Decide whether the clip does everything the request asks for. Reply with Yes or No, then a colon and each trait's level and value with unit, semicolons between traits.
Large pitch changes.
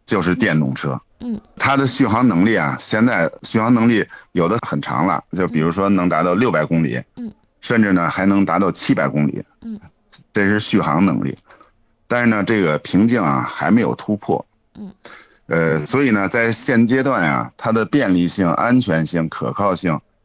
Yes: wide, 7.1 semitones